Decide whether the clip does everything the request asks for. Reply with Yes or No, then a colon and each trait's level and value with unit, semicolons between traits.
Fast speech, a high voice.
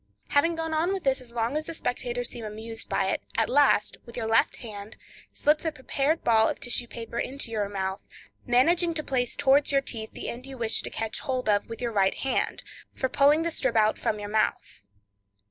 Yes: fast, 215 wpm; high, 245 Hz